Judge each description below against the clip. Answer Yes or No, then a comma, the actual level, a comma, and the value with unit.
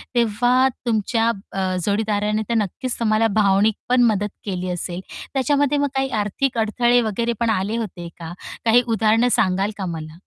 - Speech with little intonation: No, average, 3.4 semitones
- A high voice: Yes, high, 220 Hz